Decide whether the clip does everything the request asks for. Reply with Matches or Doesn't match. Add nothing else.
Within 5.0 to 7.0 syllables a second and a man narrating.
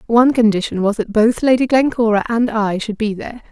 Doesn't match